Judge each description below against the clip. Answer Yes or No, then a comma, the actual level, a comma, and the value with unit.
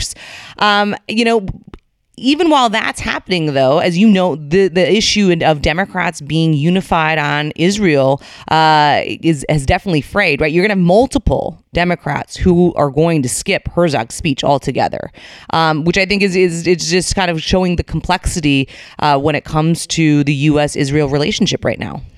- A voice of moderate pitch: Yes, medium, 165 Hz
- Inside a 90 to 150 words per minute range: No, average, 175 wpm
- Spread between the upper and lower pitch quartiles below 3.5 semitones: No, average, 3.8 semitones